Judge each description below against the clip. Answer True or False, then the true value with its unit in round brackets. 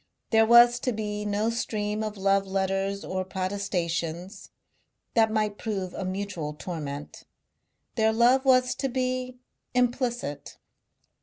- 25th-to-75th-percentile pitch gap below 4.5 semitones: True (3.9 semitones)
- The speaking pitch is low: False (210 Hz)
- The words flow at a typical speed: False (125 wpm)